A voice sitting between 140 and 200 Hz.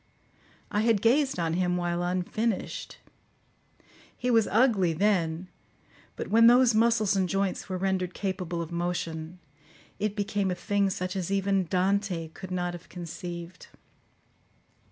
Yes: medium, 185 Hz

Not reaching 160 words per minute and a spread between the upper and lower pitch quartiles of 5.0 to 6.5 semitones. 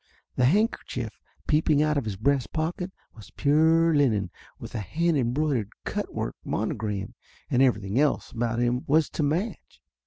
No: average, 165 wpm; average, 5.3 semitones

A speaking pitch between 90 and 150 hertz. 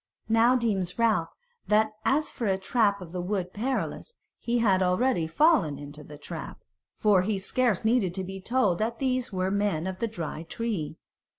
No: high, 200 Hz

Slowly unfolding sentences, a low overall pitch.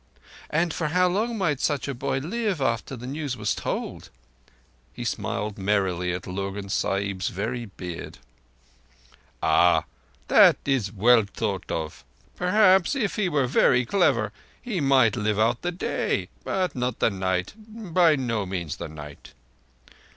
No: average, 150 wpm; low, 125 Hz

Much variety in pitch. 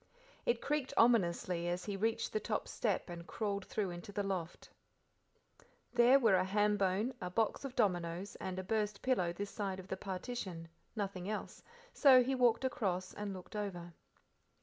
No: average, 3.7 semitones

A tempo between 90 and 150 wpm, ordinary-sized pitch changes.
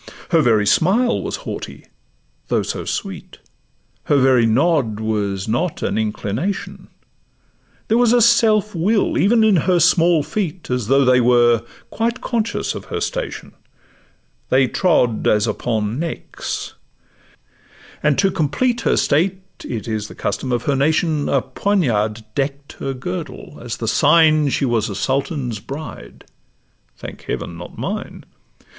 No: average, 140 wpm; wide, 7.9 semitones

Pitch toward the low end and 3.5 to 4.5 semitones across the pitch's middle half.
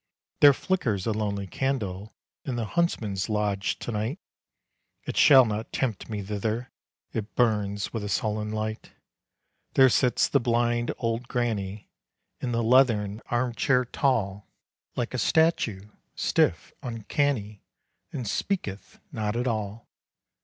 No: low, 115 Hz; average, 3.1 semitones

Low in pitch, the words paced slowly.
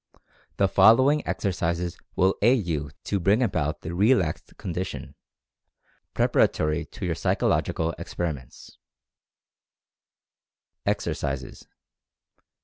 Yes: very low, 90 Hz; slow, 90 wpm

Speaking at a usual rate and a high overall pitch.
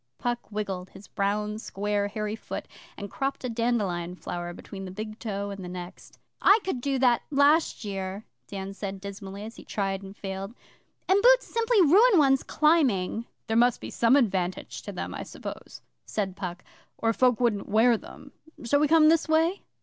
Yes: average, 180 wpm; high, 215 Hz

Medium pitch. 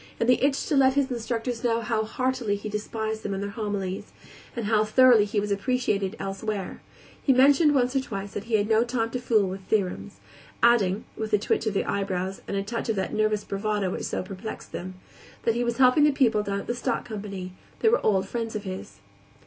No: high, 215 Hz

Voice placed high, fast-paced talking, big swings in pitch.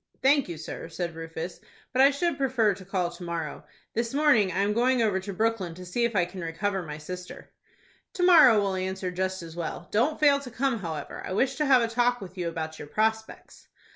Yes: high, 195 Hz; fast, 225 wpm; wide, 5.8 semitones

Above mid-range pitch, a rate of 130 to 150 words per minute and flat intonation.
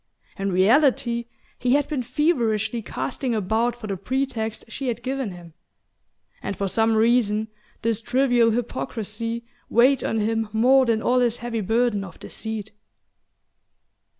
Yes: high, 230 Hz; average, 140 wpm; narrow, 2.3 semitones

